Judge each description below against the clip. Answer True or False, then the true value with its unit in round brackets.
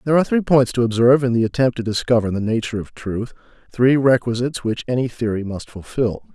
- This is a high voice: False (120 Hz)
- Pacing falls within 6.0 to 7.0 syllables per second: True (6.5 syllables/s)